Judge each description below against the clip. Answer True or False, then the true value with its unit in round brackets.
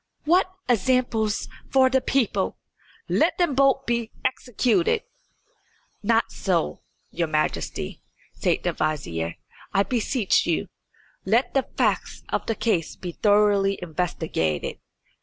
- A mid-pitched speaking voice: False (215 Hz)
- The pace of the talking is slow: True (115 wpm)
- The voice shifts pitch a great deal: True (6.8 semitones)